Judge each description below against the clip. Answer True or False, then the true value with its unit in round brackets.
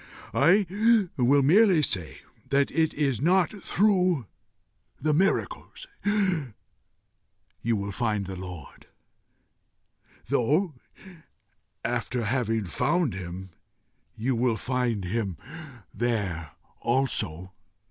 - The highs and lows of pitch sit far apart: True (7.4 semitones)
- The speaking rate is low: True (85 wpm)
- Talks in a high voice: False (120 Hz)